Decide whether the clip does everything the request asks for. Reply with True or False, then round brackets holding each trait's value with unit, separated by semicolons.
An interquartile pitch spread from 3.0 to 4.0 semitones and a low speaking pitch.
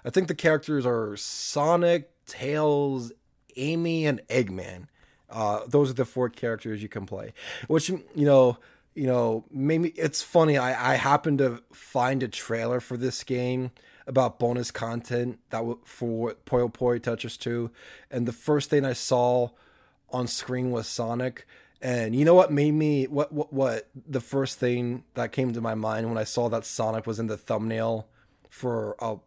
True (3.6 semitones; 125 Hz)